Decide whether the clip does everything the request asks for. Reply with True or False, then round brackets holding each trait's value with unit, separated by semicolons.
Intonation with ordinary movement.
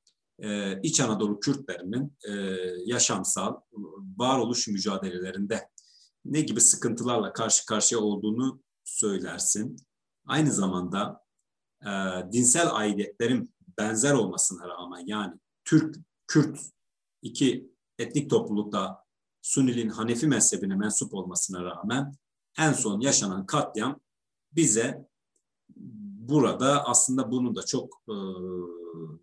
False (6.2 semitones)